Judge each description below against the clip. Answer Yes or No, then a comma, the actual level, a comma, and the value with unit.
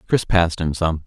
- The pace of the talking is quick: Yes, fast, 225 wpm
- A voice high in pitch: No, very low, 85 Hz